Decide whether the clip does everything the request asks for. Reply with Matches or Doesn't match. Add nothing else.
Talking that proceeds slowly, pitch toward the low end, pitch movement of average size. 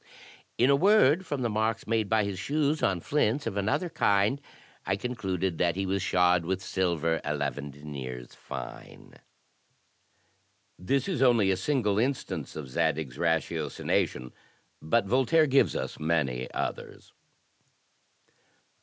Doesn't match